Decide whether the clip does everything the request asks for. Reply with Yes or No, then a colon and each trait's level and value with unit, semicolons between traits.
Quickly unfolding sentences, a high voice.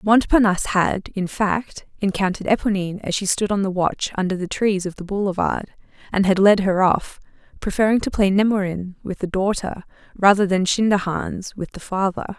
No: average, 175 wpm; high, 195 Hz